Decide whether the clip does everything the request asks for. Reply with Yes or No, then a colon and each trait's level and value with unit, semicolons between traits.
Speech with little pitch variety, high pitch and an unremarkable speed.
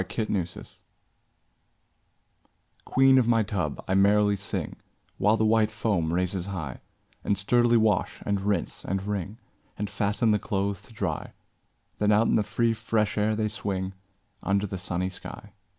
No: narrow, 2.1 semitones; low, 105 Hz; average, 155 wpm